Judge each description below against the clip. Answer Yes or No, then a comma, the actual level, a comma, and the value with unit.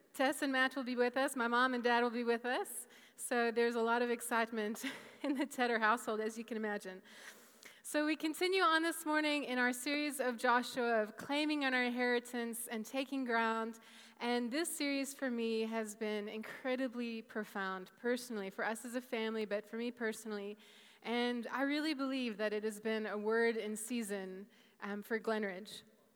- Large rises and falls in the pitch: No, narrow, 2.6 semitones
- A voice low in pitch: No, high, 235 Hz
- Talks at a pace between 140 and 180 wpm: No, average, 190 wpm